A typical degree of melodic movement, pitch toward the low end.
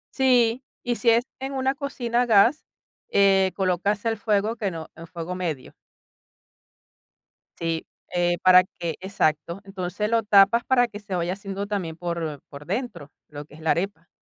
No: average, 5.0 semitones; high, 195 Hz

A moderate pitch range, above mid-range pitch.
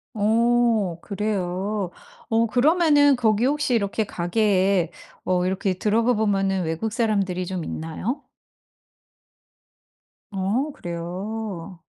Yes: average, 3.8 semitones; high, 205 Hz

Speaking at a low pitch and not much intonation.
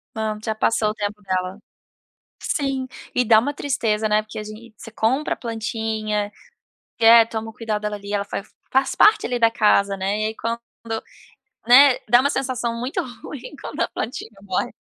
No: high, 220 Hz; narrow, 2.3 semitones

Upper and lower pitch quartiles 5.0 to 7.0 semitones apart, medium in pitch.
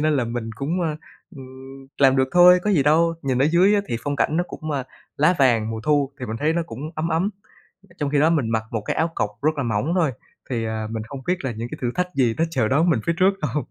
Yes: wide, 5.5 semitones; medium, 145 Hz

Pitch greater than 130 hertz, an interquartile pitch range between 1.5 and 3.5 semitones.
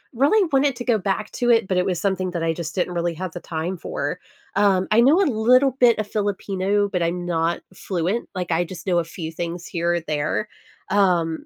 No: medium, 185 Hz; average, 3.9 semitones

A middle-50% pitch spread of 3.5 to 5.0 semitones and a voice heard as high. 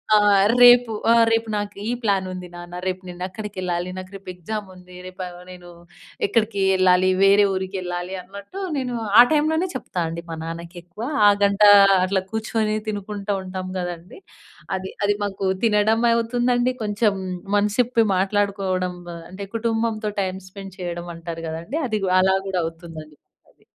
No: average, 3.0 semitones; high, 195 Hz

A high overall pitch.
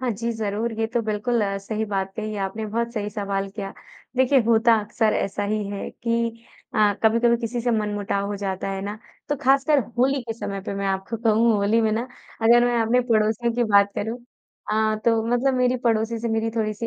Yes: high, 220 Hz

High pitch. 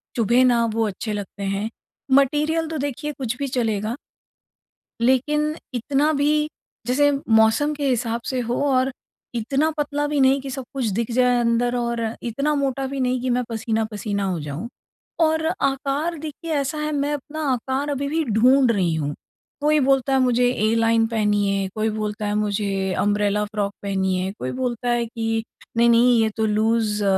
Yes: high, 240 Hz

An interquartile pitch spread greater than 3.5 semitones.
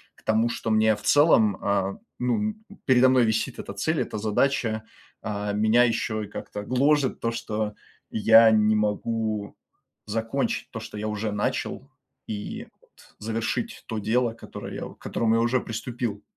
No: narrow, 2.4 semitones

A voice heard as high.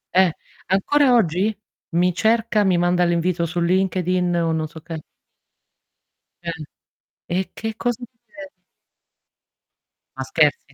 No: medium, 180 Hz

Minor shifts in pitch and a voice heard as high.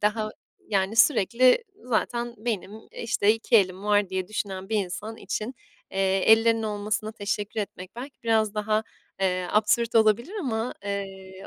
Yes: narrow, 2.3 semitones; high, 215 Hz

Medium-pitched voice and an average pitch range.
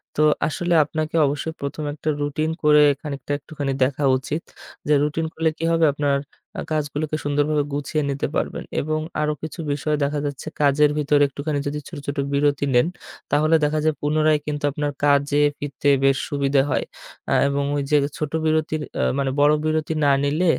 No: medium, 150 Hz; narrow, 1.4 semitones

